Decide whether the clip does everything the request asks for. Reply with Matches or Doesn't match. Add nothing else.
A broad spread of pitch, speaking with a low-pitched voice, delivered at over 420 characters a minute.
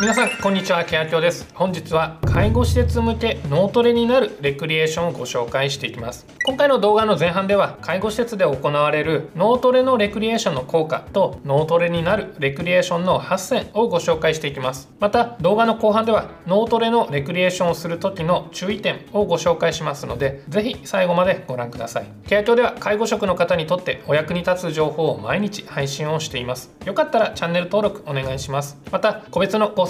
Doesn't match